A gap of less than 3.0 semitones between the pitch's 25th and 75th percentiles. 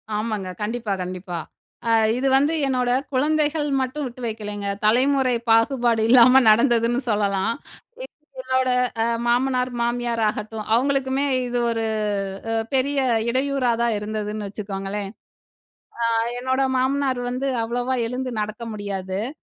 No: average, 3.5 semitones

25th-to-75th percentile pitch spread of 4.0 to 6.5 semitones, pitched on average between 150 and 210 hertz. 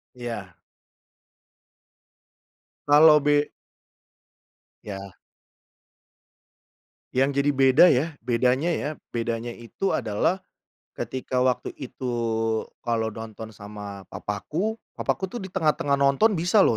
No: average, 5.0 semitones; low, 130 Hz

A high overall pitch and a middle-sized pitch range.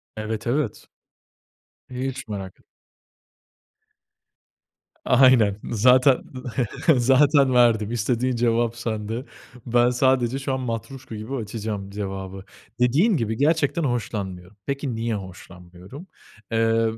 No: low, 120 Hz; average, 3.6 semitones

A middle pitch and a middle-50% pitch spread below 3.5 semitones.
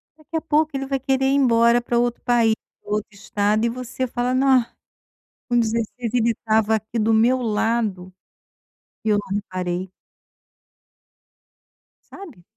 No: high, 235 Hz; average, 2.9 semitones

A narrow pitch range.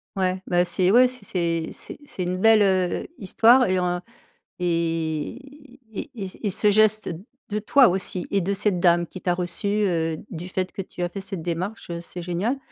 No: average, 3.3 semitones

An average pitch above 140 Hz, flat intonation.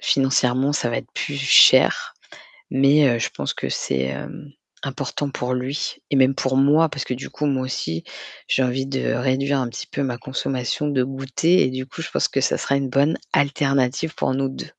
No: low, 135 Hz; narrow, 1.5 semitones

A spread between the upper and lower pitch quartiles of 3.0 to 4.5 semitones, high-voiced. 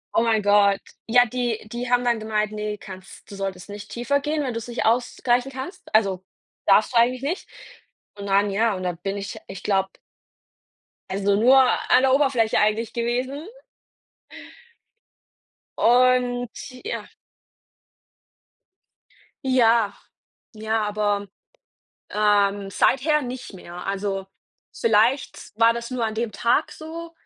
Yes: average, 3.6 semitones; high, 225 Hz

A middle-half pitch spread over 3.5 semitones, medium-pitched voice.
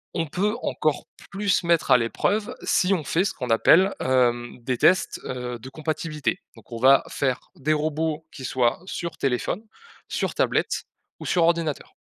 Yes: average, 5.1 semitones; medium, 150 Hz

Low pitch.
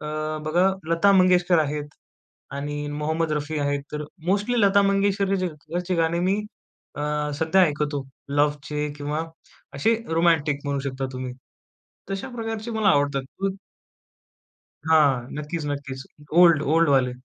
No: medium, 155 Hz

